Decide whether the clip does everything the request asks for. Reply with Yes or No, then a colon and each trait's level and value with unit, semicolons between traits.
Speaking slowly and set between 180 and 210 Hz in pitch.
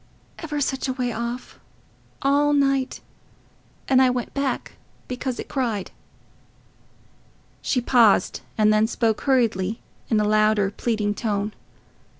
No: slow, 125 wpm; high, 240 Hz